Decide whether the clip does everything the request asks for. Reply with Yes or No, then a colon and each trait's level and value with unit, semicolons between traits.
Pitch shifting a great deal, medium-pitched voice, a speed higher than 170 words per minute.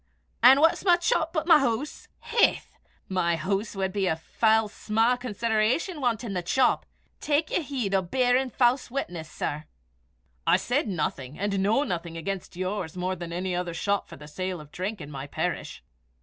No: wide, 6.0 semitones; high, 200 Hz; average, 180 wpm